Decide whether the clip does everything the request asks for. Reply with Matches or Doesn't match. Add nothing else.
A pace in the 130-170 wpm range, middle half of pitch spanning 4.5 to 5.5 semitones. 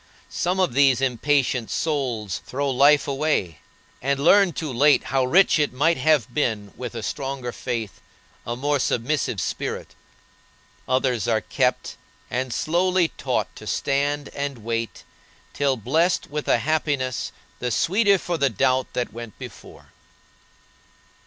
Doesn't match